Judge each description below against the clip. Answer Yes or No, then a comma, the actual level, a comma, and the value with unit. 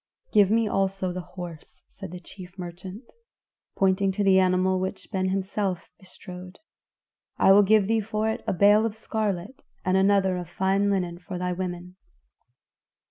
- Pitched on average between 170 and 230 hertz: Yes, high, 190 Hz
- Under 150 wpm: No, average, 165 wpm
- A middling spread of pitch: No, narrow, 1.8 semitones